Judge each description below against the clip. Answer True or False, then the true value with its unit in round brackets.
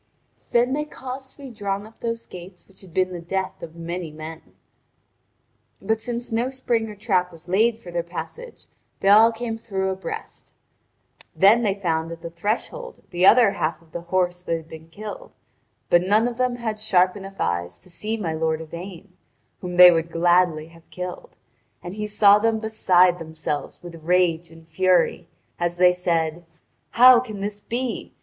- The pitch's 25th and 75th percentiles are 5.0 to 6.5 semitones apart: False (4.6 semitones)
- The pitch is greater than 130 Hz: True (185 Hz)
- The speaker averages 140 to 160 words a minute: False (180 wpm)